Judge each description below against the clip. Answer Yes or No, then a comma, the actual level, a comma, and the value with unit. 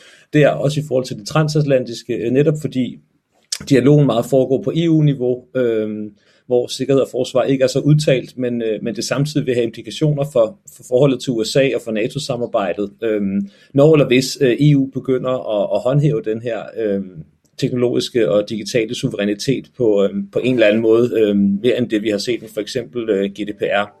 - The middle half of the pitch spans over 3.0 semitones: Yes, average, 4.2 semitones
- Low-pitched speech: Yes, low, 125 Hz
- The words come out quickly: No, average, 160 wpm